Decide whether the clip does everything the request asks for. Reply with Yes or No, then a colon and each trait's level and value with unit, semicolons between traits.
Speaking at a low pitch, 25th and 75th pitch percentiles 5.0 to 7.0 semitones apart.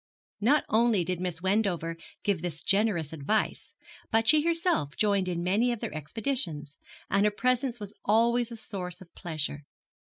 No: high, 200 Hz; average, 5.3 semitones